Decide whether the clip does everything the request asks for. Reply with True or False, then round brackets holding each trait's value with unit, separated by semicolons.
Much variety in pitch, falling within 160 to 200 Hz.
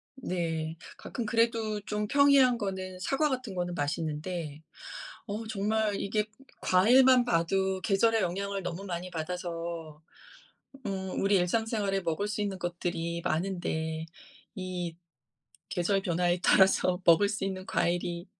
False (3.4 semitones; 190 Hz)